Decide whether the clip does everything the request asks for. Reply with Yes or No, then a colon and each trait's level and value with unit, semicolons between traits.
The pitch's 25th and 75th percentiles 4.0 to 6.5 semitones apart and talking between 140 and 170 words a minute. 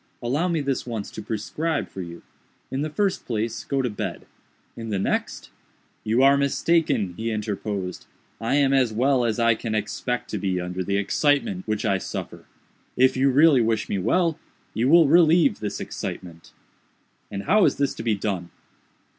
No: average, 5.3 semitones; average, 180 wpm